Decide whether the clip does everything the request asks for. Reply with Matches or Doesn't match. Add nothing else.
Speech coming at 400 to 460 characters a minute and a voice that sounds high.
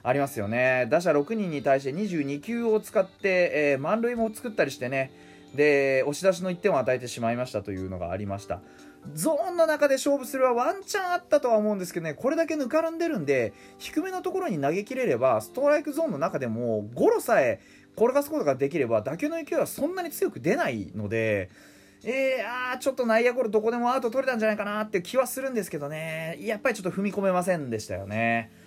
Matches